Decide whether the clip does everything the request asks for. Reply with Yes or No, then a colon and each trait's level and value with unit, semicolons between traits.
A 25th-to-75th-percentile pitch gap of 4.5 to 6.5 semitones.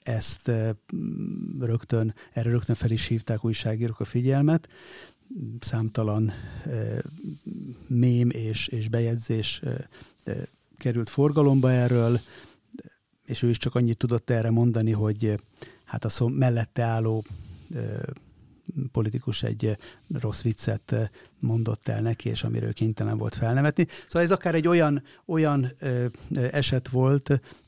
No: average, 2.9 semitones